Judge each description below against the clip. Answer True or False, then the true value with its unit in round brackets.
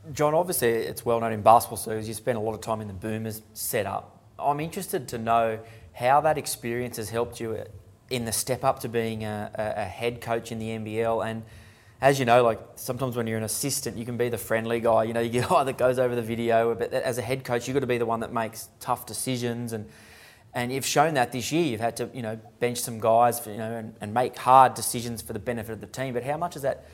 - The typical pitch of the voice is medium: False (115 Hz)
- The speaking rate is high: True (260 wpm)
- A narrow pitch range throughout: True (2.0 semitones)